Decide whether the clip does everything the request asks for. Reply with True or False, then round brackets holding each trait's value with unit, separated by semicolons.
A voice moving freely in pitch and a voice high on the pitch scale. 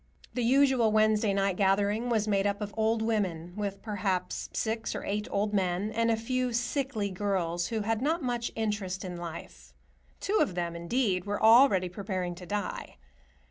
False (3.3 semitones; 210 Hz)